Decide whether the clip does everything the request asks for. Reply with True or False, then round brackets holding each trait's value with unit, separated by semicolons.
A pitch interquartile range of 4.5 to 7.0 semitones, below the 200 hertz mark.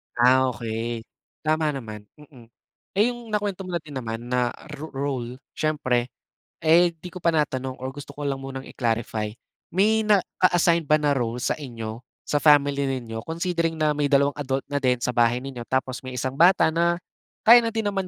True (5.0 semitones; 140 Hz)